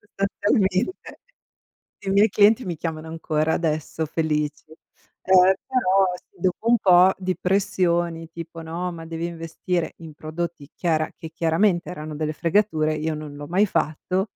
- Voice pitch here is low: No, medium, 170 Hz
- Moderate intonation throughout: Yes, average, 3.0 semitones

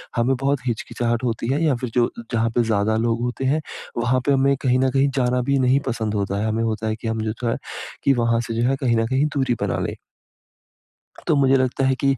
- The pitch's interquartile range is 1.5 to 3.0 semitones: Yes, average, 2.7 semitones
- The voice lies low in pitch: Yes, low, 120 Hz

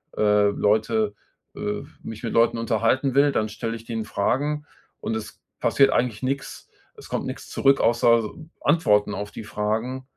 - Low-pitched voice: Yes, low, 115 Hz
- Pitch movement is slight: No, average, 3.6 semitones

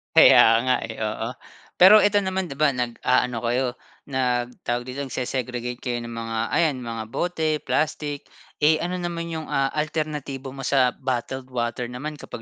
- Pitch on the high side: No, low, 130 Hz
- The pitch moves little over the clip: No, average, 4.0 semitones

